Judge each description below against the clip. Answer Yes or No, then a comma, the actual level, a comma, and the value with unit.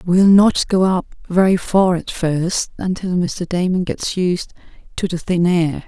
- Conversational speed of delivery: Yes, average, 175 wpm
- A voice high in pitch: No, medium, 180 Hz